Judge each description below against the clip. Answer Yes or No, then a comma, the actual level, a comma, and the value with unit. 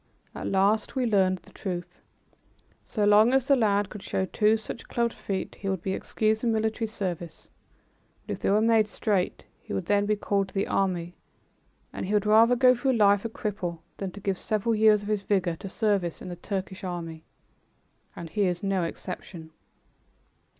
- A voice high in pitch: Yes, high, 200 Hz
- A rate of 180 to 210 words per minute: Yes, average, 190 wpm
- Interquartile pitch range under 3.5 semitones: Yes, average, 2.7 semitones